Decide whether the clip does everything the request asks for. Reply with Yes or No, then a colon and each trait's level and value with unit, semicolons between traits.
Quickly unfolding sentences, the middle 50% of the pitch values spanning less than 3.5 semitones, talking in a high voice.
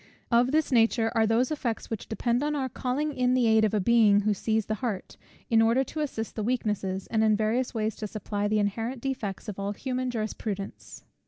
Yes: fast, 215 wpm; average, 2.9 semitones; high, 225 Hz